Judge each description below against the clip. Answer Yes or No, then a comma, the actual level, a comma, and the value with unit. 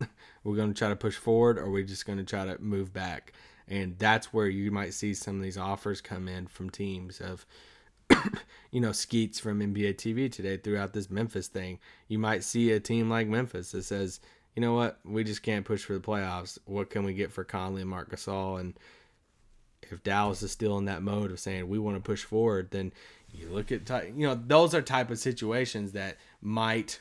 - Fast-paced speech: Yes, fast, 220 wpm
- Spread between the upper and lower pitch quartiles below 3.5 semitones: Yes, narrow, 2.4 semitones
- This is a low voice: Yes, low, 100 Hz